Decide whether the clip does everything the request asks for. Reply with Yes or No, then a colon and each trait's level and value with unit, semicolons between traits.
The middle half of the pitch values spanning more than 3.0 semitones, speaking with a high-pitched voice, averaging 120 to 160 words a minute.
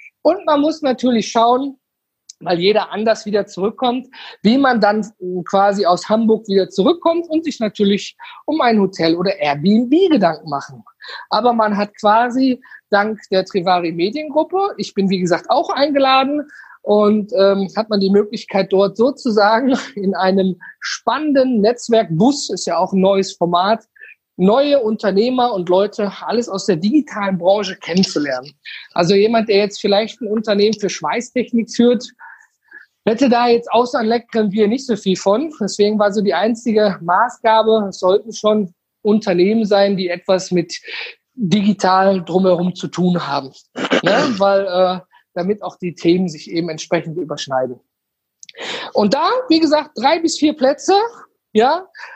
Yes: average, 4.4 semitones; high, 210 Hz; average, 150 wpm